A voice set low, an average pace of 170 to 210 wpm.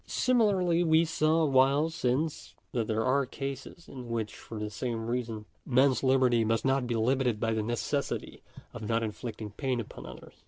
Yes: low, 125 Hz; average, 185 wpm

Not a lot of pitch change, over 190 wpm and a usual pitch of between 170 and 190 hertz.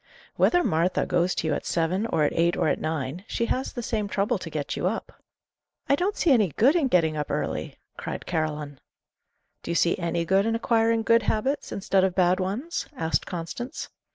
No: wide, 5.6 semitones; fast, 205 wpm; medium, 185 Hz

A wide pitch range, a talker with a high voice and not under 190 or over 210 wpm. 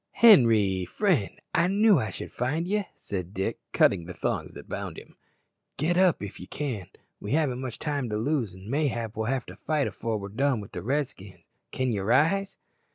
No: wide, 7.1 semitones; low, 125 Hz; average, 195 wpm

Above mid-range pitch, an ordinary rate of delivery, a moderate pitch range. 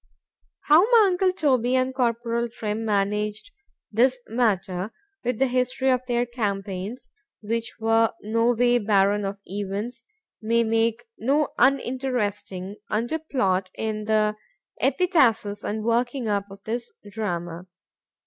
No: high, 230 Hz; slow, 120 wpm; average, 3.5 semitones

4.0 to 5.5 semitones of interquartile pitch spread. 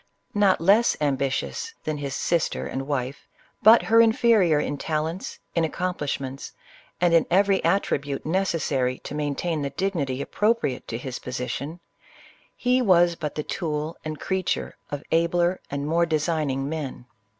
Yes: average, 4.5 semitones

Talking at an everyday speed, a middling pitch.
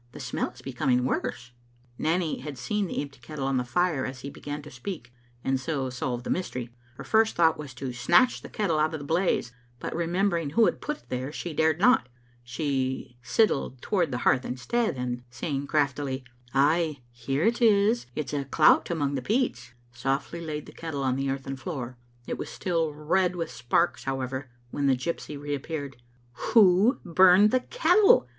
Yes: average, 185 wpm; medium, 145 Hz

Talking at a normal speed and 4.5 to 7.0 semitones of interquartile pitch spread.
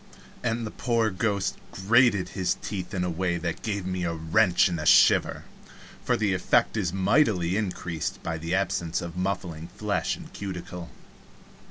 No: average, 165 wpm; average, 3.1 semitones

